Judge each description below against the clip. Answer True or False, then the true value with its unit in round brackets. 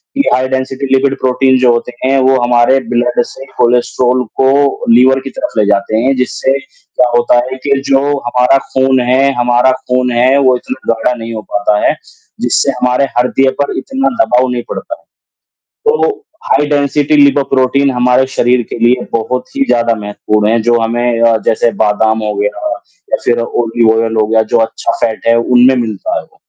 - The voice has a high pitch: False (125 Hz)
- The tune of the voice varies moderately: False (2.2 semitones)